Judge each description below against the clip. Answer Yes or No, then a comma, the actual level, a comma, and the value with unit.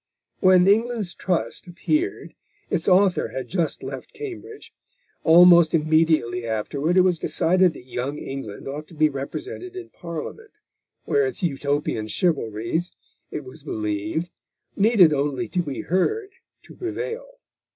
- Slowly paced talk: Yes, slow, 130 wpm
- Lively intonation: Yes, wide, 6.1 semitones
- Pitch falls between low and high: Yes, medium, 170 Hz